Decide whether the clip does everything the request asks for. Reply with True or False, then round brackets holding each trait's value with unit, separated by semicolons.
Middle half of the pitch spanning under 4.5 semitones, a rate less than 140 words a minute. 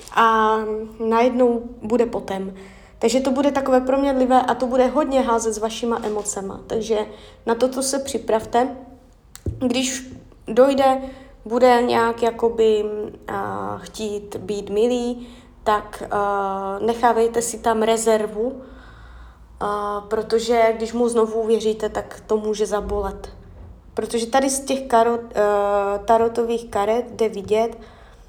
True (2.4 semitones; 120 wpm)